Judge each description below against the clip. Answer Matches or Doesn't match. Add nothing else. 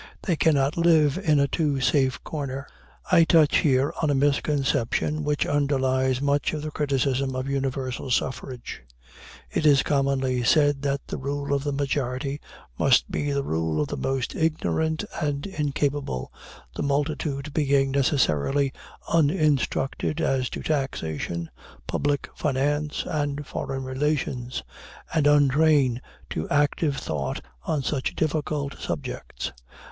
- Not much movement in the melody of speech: Matches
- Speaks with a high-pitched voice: Doesn't match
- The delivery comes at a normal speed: Doesn't match